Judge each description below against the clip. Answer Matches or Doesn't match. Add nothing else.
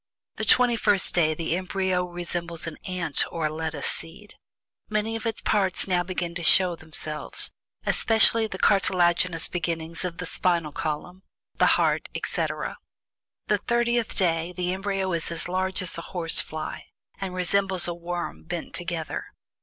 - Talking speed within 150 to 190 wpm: Matches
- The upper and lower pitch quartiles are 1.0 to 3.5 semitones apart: Matches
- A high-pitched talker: Doesn't match